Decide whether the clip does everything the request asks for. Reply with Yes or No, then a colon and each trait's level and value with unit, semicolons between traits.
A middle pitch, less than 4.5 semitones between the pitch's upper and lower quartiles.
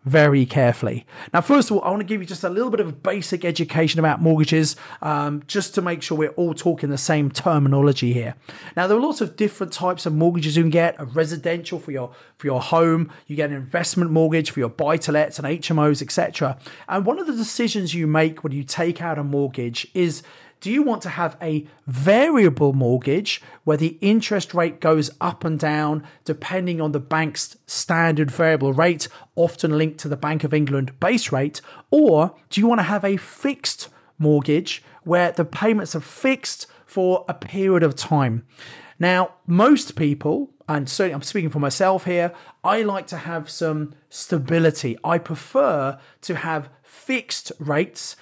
Yes: medium, 165 Hz; average, 3.5 semitones